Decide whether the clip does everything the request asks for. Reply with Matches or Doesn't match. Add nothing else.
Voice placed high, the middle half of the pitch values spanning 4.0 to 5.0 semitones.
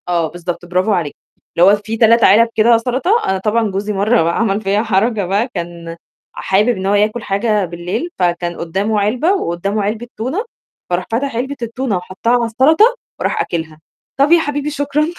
Matches